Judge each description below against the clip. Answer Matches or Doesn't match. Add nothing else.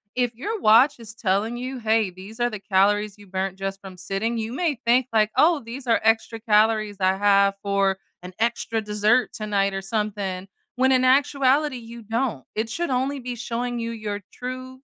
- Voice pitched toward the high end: Matches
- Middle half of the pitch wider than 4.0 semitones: Doesn't match